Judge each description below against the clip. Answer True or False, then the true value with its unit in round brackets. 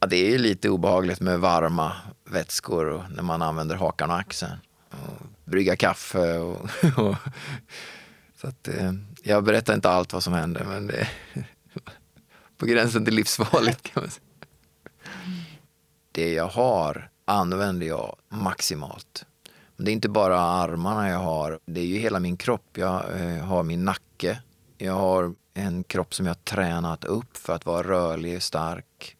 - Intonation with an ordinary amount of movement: True (3.6 semitones)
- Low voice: True (90 Hz)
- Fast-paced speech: False (160 wpm)